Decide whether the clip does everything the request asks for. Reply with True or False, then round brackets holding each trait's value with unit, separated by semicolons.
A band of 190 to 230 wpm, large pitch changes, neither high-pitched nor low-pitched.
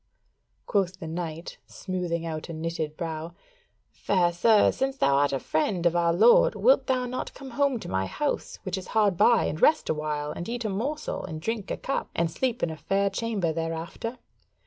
True (195 wpm; 6.2 semitones; 180 Hz)